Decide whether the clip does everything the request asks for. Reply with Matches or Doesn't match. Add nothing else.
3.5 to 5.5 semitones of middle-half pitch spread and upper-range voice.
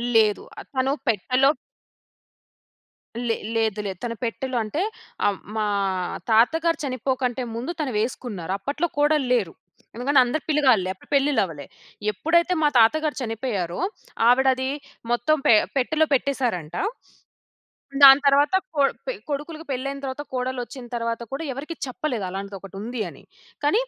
Matches